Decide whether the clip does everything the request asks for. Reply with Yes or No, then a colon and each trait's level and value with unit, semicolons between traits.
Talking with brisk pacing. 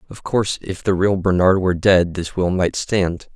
Yes: fast, 215 wpm